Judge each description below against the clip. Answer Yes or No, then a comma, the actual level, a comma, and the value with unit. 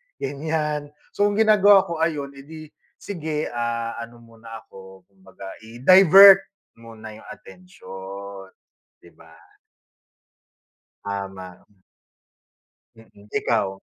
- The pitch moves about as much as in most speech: No, wide, 8.2 semitones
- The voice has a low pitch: Yes, low, 120 Hz